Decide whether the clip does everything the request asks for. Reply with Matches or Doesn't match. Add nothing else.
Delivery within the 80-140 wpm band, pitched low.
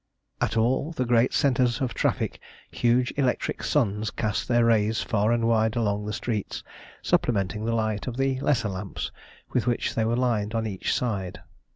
Doesn't match